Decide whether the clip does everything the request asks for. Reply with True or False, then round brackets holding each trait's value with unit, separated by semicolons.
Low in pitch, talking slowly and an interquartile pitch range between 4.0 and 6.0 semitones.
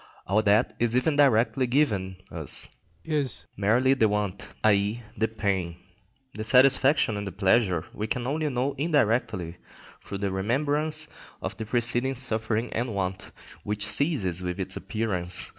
False (110 Hz; 145 wpm; 4.6 semitones)